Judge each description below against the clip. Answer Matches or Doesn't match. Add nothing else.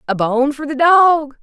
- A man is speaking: Doesn't match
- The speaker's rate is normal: Doesn't match